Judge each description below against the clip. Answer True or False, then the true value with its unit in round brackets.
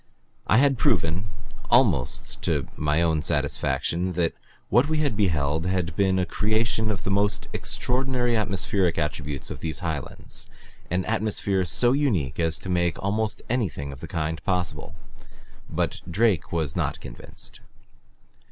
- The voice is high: False (90 Hz)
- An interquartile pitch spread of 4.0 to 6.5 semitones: True (5.5 semitones)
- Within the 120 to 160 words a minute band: True (140 wpm)